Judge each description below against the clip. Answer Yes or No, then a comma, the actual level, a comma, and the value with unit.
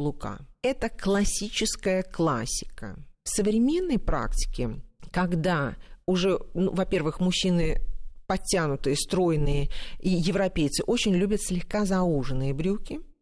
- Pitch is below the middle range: No, medium, 185 Hz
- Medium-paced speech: No, slow, 95 wpm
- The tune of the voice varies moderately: Yes, average, 5.0 semitones